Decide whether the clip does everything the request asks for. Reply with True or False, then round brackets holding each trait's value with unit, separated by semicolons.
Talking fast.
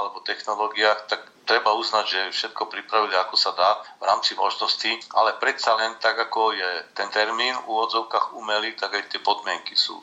True (180 wpm)